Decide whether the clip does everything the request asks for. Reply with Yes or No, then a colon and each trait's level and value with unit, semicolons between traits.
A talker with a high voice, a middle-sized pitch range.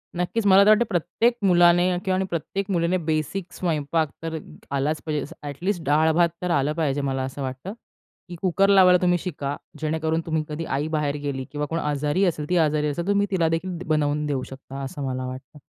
No: medium, 160 Hz; average, 3.7 semitones